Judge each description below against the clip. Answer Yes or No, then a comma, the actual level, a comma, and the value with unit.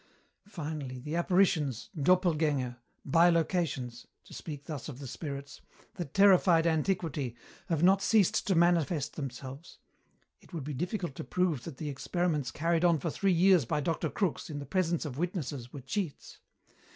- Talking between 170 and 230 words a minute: No, average, 155 wpm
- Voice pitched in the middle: Yes, medium, 160 Hz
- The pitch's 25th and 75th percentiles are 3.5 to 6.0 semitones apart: Yes, average, 4.1 semitones